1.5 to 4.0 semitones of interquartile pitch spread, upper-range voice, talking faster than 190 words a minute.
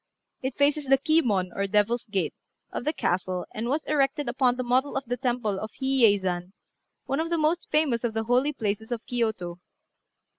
No: average, 4.7 semitones; high, 245 Hz; average, 200 wpm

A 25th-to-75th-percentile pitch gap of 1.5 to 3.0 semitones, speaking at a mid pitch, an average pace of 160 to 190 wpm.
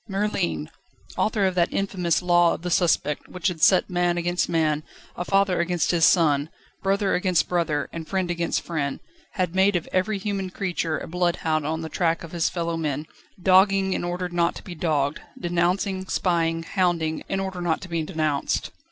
Yes: narrow, 2.4 semitones; medium, 175 Hz; average, 180 wpm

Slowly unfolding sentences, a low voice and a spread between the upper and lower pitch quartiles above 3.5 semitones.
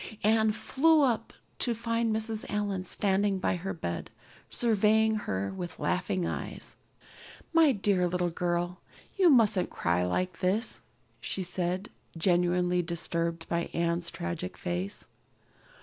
No: slow, 125 wpm; medium, 185 Hz; average, 4.2 semitones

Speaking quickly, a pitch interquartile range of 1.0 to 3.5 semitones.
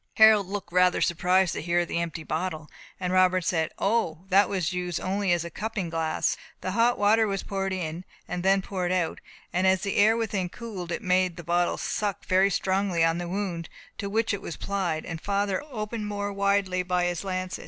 Yes: fast, 210 wpm; narrow, 2.4 semitones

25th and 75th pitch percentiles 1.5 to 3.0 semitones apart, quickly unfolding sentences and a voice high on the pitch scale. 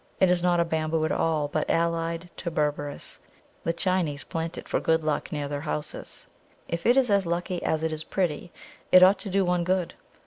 No: narrow, 2.4 semitones; fast, 210 wpm; medium, 165 Hz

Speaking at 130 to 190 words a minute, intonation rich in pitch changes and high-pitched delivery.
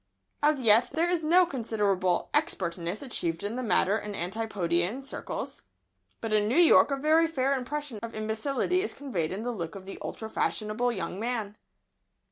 Yes: average, 170 wpm; wide, 5.7 semitones; high, 225 Hz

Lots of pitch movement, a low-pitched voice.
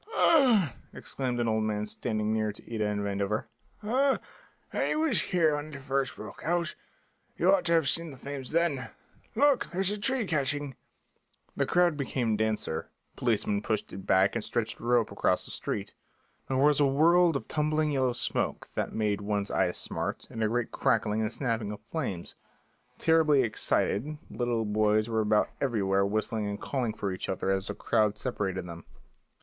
Yes: wide, 6.4 semitones; low, 120 Hz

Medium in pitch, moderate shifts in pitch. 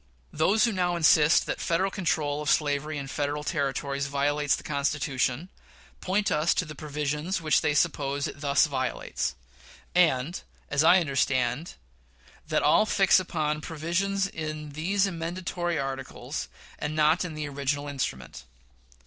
Yes: medium, 150 Hz; average, 3.4 semitones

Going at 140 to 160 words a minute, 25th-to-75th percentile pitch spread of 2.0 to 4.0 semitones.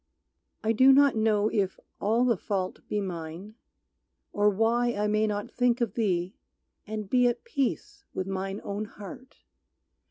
Yes: average, 155 wpm; average, 3.5 semitones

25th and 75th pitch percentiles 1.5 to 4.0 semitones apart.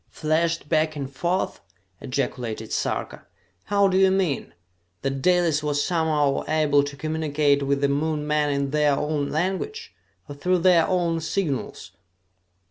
Yes: average, 3.2 semitones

